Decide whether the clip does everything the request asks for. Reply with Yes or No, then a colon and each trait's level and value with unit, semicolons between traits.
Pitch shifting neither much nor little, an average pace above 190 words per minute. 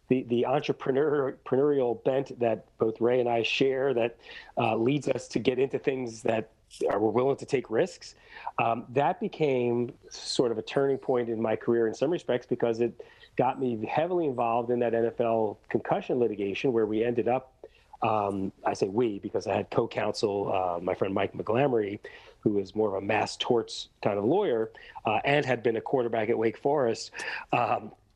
No: average, 3.3 semitones; average, 185 wpm